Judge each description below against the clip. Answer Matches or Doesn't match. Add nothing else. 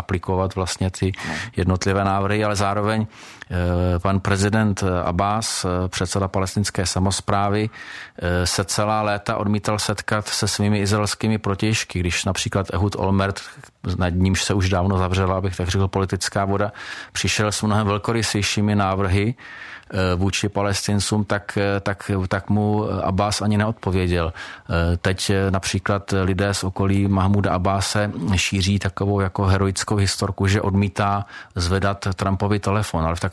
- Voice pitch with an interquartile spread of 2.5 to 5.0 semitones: Doesn't match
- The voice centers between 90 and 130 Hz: Matches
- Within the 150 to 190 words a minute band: Doesn't match